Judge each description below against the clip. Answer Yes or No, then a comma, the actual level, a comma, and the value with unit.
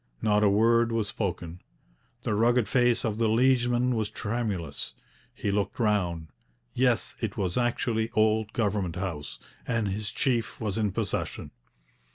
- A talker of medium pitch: No, low, 110 Hz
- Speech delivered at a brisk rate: No, average, 145 wpm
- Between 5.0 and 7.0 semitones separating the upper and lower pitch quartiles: No, average, 2.7 semitones